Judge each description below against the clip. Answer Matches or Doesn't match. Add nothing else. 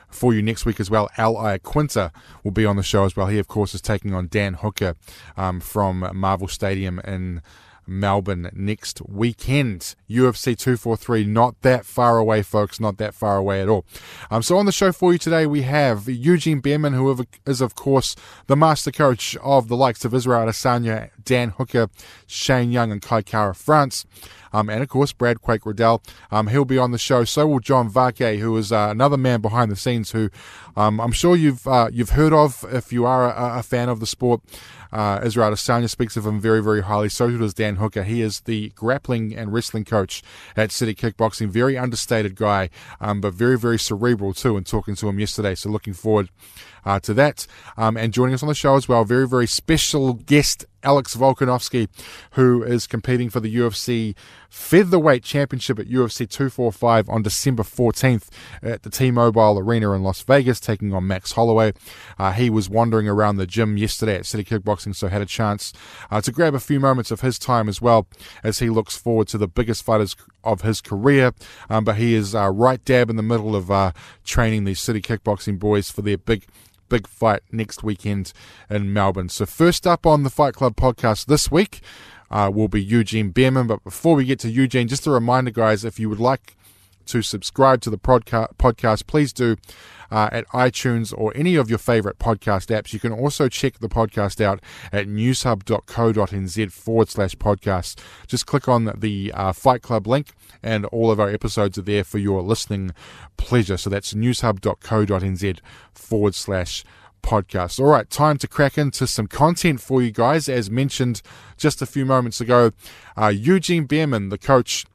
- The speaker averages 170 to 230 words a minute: Matches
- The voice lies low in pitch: Matches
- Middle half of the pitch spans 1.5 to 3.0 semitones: Doesn't match